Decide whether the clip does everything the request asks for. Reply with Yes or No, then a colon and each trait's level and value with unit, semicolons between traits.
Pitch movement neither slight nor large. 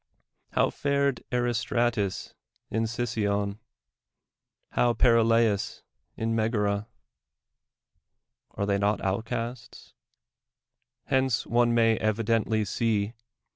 No: narrow, 2.3 semitones